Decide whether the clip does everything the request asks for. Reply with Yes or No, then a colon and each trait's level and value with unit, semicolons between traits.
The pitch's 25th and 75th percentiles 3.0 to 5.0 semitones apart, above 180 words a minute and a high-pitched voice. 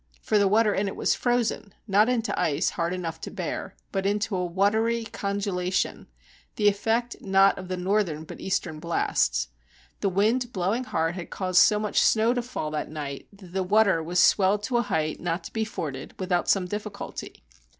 Yes: average, 3.4 semitones; average, 190 wpm; high, 195 Hz